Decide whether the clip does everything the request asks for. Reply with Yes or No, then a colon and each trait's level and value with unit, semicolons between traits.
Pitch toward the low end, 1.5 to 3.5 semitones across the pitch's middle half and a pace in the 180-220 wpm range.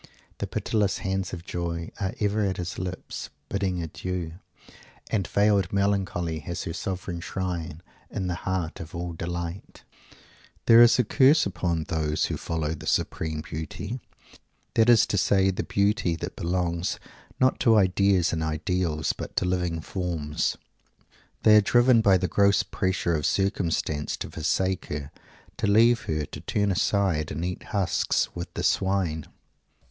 No: very low, 90 Hz; average, 3.1 semitones; average, 155 wpm